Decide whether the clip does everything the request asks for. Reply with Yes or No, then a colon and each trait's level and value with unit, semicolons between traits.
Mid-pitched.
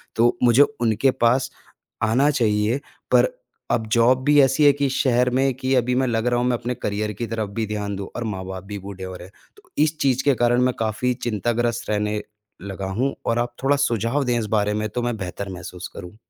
No: low, 120 Hz